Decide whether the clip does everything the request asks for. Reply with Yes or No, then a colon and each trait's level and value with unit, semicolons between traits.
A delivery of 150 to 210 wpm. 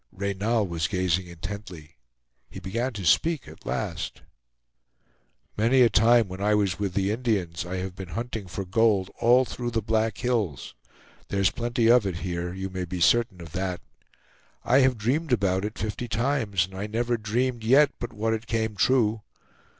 Yes: average, 175 wpm